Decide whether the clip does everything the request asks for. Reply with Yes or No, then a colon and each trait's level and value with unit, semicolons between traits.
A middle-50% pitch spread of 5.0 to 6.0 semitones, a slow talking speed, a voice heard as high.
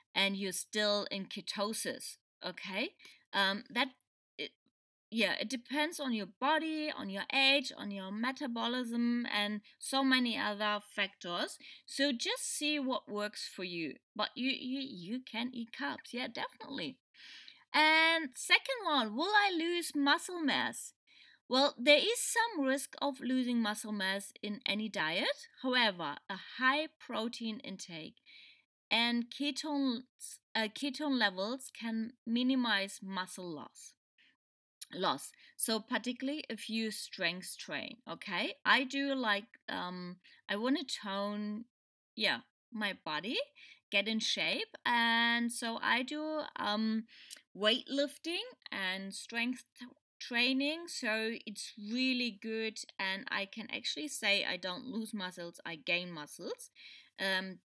Yes: wide, 5.4 semitones; slow, 130 wpm; high, 235 Hz